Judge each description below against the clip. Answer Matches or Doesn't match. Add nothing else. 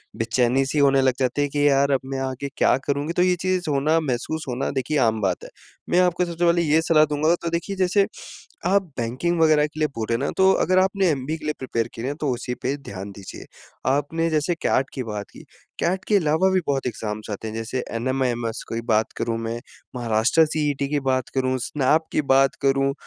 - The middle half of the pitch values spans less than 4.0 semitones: Doesn't match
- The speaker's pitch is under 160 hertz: Matches